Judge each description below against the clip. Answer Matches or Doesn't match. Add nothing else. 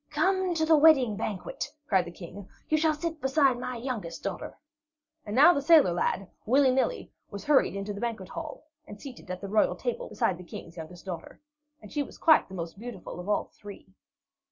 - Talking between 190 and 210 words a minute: Matches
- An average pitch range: Doesn't match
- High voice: Matches